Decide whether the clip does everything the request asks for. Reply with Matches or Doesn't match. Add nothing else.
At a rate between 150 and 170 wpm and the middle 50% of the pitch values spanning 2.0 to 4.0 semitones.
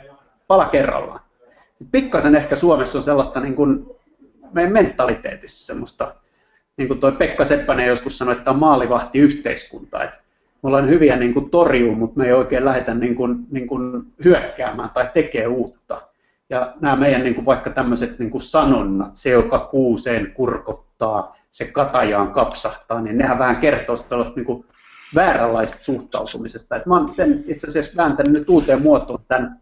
Doesn't match